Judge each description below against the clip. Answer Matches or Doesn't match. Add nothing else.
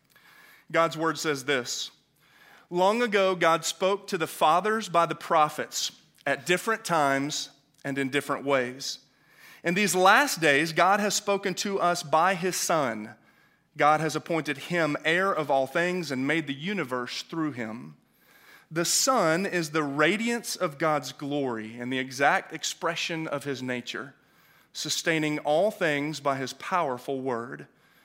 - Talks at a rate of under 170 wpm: Matches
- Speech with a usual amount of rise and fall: Matches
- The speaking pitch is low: Doesn't match